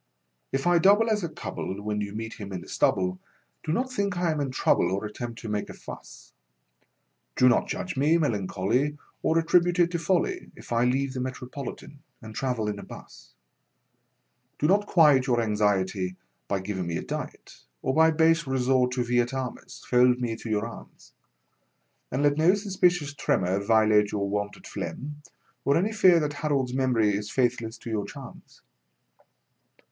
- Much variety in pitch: Yes, wide, 7.1 semitones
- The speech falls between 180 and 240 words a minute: Yes, average, 185 wpm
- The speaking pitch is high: No, low, 125 Hz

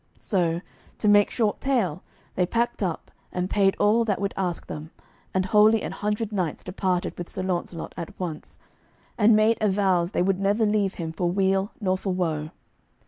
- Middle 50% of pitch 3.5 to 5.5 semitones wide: No, average, 2.8 semitones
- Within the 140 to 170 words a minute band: No, average, 180 wpm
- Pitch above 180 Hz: Yes, high, 190 Hz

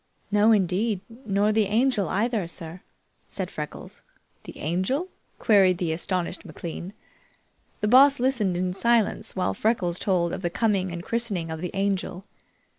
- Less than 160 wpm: Yes, average, 145 wpm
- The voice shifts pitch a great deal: No, average, 3.8 semitones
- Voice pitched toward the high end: Yes, high, 195 Hz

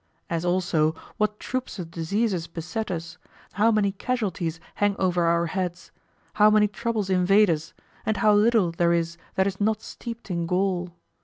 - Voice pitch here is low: No, high, 190 Hz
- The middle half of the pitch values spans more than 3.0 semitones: Yes, average, 3.8 semitones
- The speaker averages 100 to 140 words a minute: No, average, 165 wpm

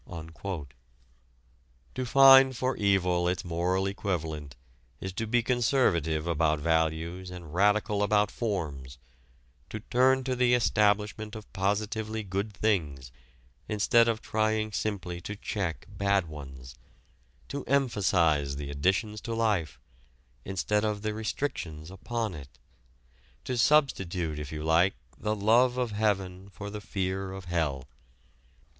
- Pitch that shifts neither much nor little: Yes, average, 4.7 semitones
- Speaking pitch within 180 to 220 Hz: No, low, 100 Hz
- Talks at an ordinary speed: No, slow, 125 wpm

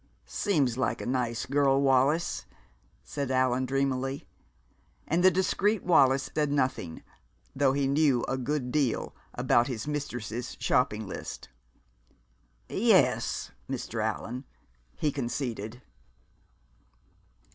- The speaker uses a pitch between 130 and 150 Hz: Yes, low, 135 Hz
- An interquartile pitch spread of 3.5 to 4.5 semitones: No, average, 2.7 semitones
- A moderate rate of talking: No, slow, 105 wpm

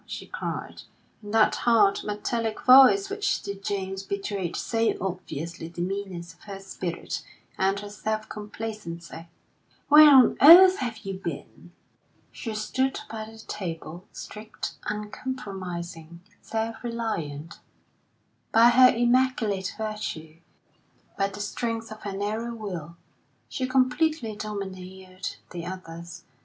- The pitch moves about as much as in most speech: Yes, average, 3.7 semitones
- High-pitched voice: Yes, high, 205 Hz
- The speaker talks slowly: Yes, slow, 120 wpm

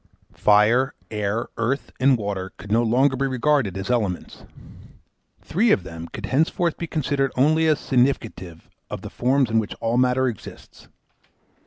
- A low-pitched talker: Yes, low, 125 Hz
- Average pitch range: Yes, average, 4.6 semitones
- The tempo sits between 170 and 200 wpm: No, average, 155 wpm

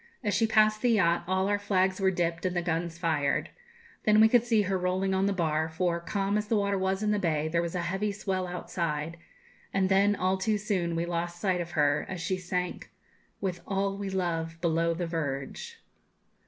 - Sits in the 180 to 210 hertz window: Yes, medium, 185 Hz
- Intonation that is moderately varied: Yes, average, 3.0 semitones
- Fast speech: Yes, fast, 215 wpm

